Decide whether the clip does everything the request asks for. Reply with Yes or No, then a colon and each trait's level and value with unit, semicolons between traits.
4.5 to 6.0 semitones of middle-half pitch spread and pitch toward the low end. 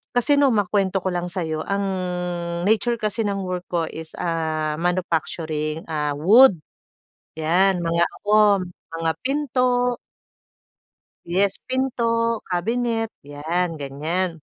No: wide, 5.5 semitones; medium, 185 Hz